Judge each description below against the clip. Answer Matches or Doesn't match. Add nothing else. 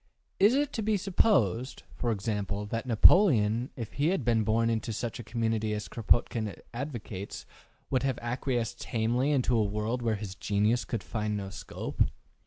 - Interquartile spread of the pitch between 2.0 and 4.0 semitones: Matches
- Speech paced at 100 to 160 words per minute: Doesn't match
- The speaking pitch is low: Matches